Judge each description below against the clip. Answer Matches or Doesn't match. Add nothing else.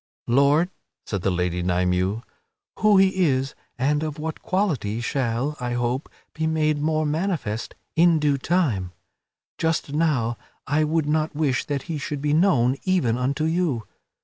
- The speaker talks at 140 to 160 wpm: Matches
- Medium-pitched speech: Matches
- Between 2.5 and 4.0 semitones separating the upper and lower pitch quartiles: Doesn't match